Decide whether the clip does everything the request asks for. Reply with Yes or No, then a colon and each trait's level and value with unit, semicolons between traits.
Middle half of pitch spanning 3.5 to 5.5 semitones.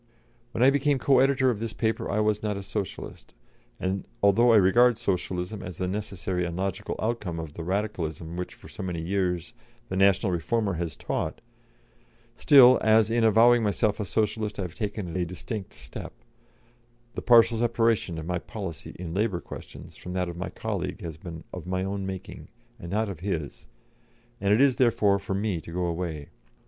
Yes: average, 3.9 semitones